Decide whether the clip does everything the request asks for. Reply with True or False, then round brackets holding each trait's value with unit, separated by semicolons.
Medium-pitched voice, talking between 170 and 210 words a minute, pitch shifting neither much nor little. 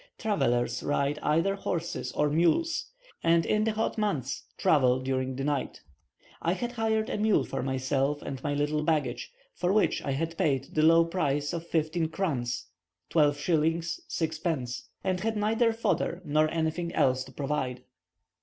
False (155 Hz; 155 wpm; 4.5 semitones)